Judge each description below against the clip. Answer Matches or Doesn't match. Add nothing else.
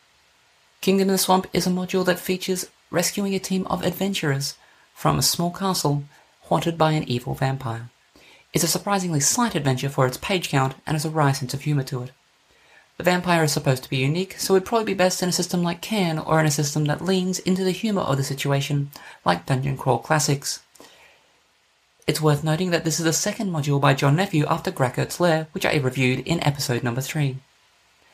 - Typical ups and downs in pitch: Matches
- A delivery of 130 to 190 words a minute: Doesn't match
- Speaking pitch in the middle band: Matches